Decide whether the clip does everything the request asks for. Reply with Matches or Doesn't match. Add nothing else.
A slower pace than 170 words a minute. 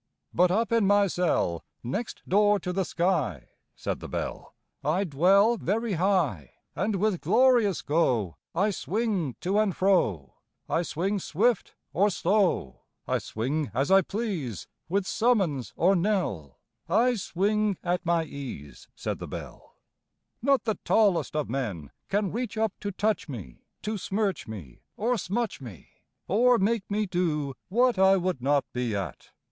Matches